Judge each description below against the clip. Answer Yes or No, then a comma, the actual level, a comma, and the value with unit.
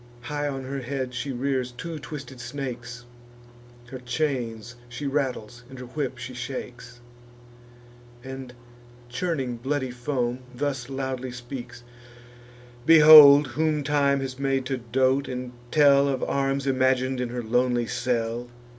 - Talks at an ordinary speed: No, slow, 130 wpm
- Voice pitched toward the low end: Yes, low, 130 Hz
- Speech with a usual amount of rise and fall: No, narrow, 2.2 semitones